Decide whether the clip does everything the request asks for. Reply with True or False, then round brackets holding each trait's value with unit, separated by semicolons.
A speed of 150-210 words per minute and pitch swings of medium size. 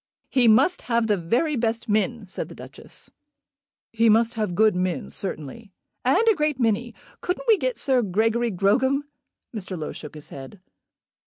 True (165 wpm; 4.2 semitones)